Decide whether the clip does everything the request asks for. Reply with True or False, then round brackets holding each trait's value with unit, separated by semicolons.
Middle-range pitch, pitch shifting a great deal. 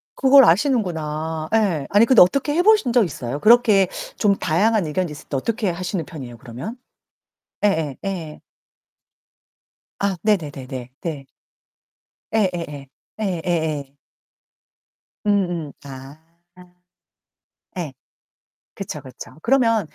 True (175 Hz; 6.1 semitones)